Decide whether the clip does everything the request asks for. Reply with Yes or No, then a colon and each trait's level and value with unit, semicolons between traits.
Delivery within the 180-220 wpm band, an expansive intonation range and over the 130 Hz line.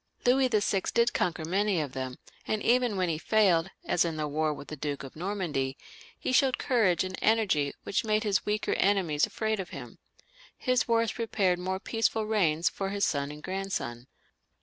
Yes: average, 185 wpm; wide, 5.8 semitones; high, 190 Hz